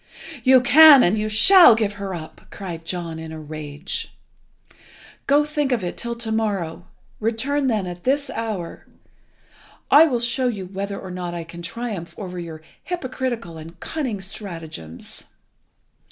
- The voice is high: Yes, high, 200 Hz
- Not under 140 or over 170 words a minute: Yes, average, 155 wpm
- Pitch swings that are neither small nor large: No, wide, 6.3 semitones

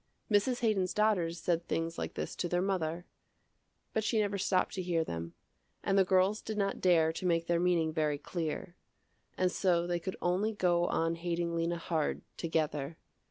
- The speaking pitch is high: No, medium, 175 Hz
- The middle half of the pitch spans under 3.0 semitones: Yes, narrow, 2.5 semitones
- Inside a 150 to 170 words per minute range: No, average, 180 wpm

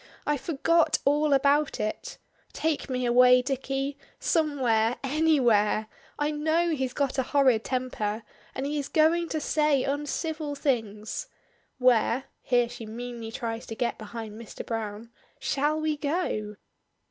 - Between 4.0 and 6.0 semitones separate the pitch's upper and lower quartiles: Yes, average, 4.3 semitones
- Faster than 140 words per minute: No, slow, 135 wpm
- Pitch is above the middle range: Yes, very high, 270 Hz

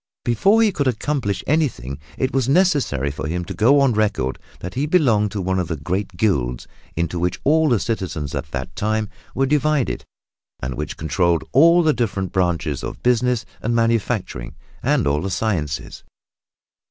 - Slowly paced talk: No, average, 170 wpm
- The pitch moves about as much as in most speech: No, wide, 8.2 semitones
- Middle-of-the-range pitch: No, low, 105 Hz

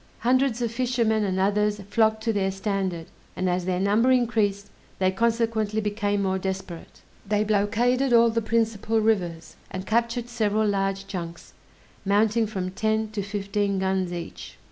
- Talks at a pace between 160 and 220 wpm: No, average, 150 wpm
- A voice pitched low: No, high, 210 Hz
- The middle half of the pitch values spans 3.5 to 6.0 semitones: No, average, 2.7 semitones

